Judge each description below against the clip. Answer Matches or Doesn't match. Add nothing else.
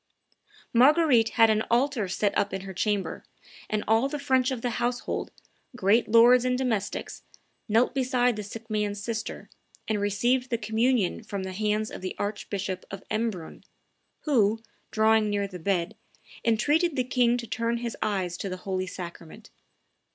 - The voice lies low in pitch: Doesn't match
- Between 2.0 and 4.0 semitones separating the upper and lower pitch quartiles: Matches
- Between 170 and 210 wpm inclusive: Doesn't match